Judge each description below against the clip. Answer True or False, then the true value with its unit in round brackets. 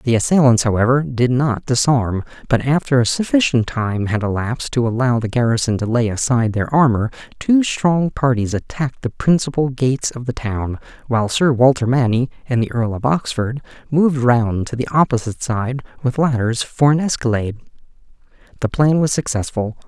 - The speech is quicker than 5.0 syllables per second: True (5.3 syllables/s)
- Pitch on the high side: False (125 Hz)